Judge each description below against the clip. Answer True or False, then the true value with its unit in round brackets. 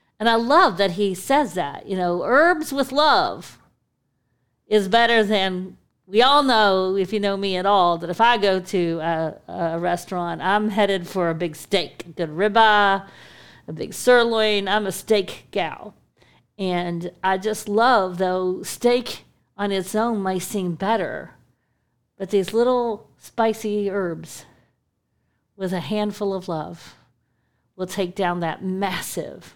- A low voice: False (195 Hz)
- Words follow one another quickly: False (150 wpm)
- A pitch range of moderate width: True (3.6 semitones)